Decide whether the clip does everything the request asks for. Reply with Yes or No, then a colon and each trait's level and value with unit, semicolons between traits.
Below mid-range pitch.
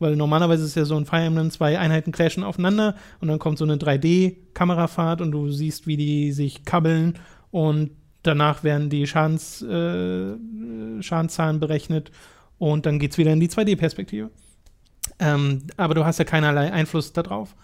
No: medium, 155 Hz